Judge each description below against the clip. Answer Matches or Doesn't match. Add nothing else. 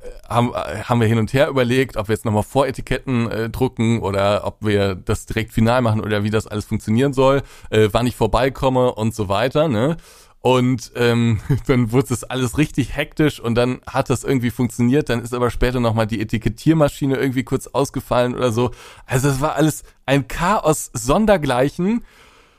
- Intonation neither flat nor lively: Matches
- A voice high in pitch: Doesn't match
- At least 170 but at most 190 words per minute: Matches